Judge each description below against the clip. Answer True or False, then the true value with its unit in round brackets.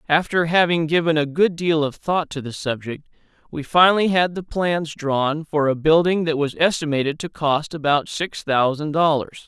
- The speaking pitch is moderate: True (155 Hz)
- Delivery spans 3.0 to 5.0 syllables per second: True (4.7 syllables/s)